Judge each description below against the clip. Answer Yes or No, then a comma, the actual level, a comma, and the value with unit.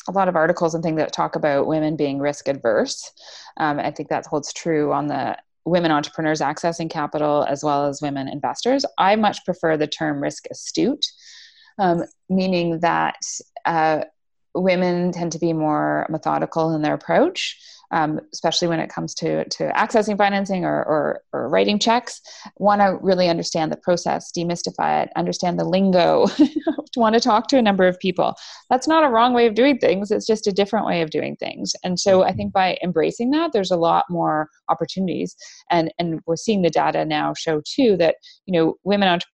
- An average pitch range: Yes, average, 4.9 semitones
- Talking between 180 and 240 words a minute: Yes, average, 190 wpm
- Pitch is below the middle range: No, medium, 180 Hz